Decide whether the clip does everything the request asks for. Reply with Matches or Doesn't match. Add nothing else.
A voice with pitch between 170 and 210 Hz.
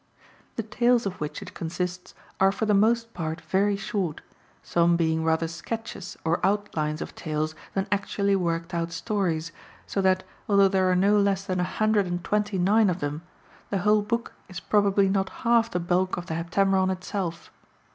Matches